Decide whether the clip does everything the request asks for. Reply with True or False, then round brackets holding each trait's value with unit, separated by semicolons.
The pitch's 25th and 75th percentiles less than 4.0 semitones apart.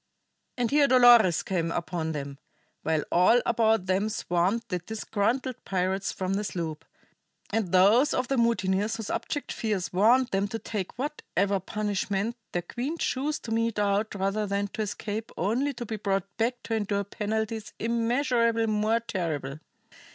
True (3.5 semitones)